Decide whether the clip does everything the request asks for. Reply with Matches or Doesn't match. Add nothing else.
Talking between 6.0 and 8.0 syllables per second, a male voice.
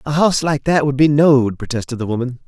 Matches